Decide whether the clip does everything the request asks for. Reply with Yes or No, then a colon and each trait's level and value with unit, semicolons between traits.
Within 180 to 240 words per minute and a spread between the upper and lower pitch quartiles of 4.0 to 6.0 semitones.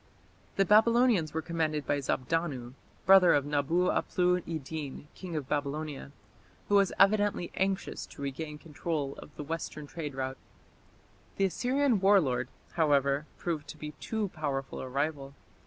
No: average, 145 wpm; average, 4.5 semitones